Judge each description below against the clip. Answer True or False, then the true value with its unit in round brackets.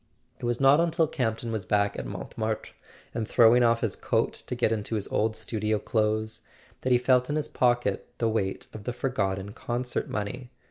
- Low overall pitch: True (115 Hz)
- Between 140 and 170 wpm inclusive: False (195 wpm)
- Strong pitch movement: False (2.6 semitones)